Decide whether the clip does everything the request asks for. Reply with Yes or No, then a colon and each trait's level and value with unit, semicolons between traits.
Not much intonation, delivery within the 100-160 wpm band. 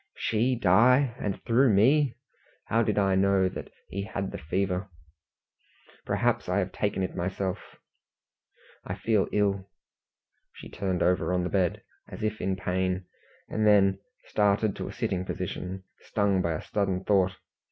Yes: narrow, 2.3 semitones; average, 150 wpm